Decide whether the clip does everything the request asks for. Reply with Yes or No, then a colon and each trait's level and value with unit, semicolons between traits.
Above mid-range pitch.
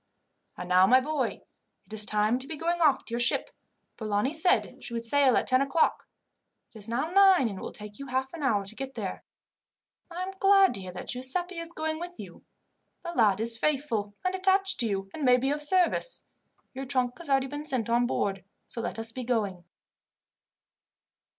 Yes: very high, 260 Hz